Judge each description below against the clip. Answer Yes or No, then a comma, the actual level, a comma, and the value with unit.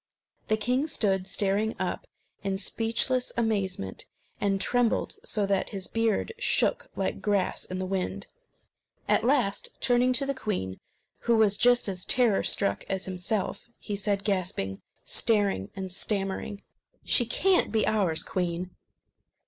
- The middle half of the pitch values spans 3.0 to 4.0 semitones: Yes, average, 3.4 semitones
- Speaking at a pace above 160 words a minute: No, average, 140 wpm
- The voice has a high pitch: Yes, high, 200 Hz